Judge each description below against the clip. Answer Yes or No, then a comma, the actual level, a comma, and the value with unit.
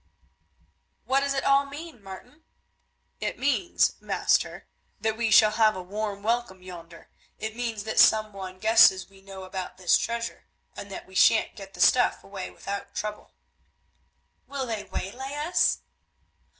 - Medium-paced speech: Yes, average, 150 wpm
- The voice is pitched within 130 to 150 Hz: No, high, 215 Hz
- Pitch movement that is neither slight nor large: Yes, average, 4.1 semitones